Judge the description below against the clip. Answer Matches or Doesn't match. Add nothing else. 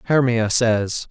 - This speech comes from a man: Matches